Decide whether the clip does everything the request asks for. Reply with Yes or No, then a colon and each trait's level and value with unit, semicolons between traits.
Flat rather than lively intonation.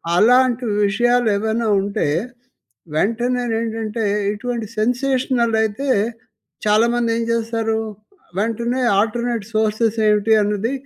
Yes: narrow, 1.9 semitones